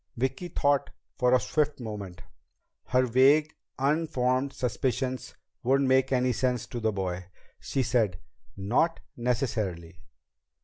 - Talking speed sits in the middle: No, slow, 120 wpm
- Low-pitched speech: Yes, low, 125 Hz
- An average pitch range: Yes, average, 3.4 semitones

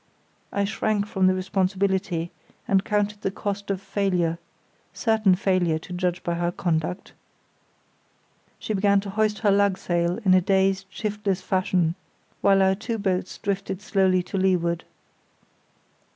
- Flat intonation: Yes, narrow, 1.8 semitones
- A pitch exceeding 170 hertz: Yes, high, 190 Hz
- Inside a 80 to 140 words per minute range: Yes, slow, 135 wpm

